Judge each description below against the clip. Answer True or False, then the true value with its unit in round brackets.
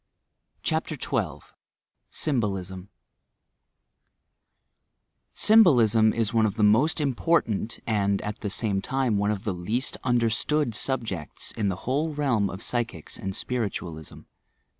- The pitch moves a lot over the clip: False (4.2 semitones)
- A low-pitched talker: True (110 Hz)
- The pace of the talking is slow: True (120 wpm)